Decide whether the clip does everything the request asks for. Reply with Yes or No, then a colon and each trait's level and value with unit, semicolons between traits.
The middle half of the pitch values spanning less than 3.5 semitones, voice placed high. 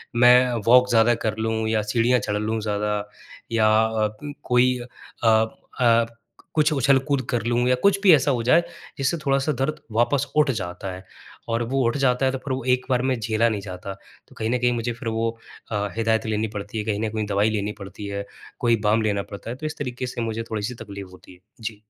No: average, 2.9 semitones; low, 115 Hz